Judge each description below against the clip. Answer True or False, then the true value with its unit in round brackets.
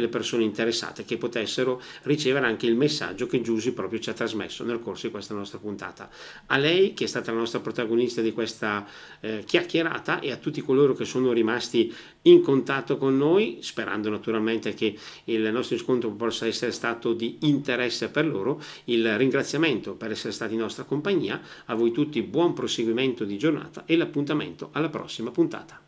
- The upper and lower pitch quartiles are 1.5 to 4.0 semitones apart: True (3.4 semitones)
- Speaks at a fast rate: True (180 wpm)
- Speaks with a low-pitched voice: True (115 Hz)